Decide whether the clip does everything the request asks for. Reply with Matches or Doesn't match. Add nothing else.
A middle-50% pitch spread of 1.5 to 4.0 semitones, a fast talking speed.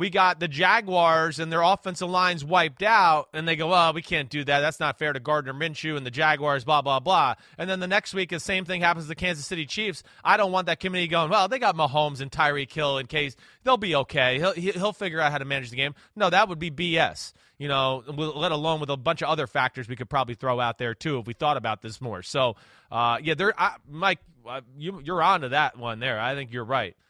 Doesn't match